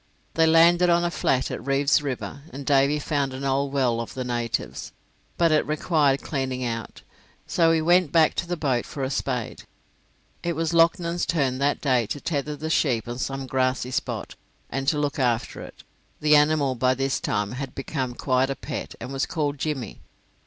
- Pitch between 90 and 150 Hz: Yes, medium, 140 Hz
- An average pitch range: Yes, average, 3.3 semitones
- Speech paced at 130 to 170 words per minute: No, average, 190 wpm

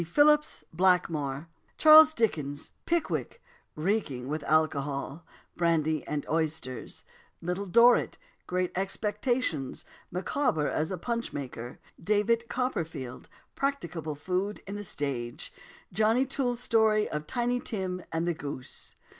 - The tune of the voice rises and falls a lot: Yes, wide, 7.3 semitones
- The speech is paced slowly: Yes, slow, 115 wpm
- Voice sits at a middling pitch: Yes, medium, 180 Hz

